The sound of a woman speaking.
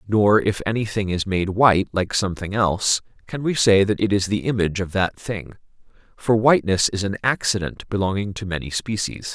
No: male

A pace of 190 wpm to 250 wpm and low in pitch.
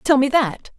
No: fast, 230 wpm; very high, 265 Hz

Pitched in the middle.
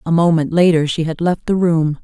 Yes: medium, 165 Hz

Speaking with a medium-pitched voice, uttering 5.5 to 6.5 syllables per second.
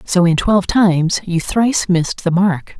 No: medium, 180 Hz; 4.9 syllables/s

